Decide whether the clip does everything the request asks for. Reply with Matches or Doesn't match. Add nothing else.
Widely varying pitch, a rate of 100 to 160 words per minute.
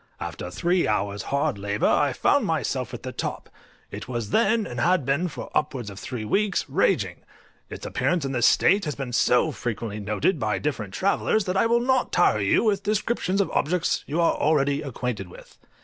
Doesn't match